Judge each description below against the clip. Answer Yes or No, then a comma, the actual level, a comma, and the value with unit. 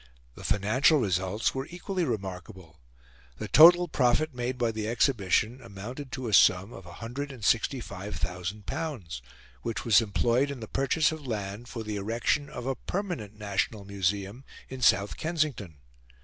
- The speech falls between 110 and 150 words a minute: Yes, average, 140 wpm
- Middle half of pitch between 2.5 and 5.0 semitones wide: No, wide, 5.4 semitones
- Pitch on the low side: Yes, low, 115 Hz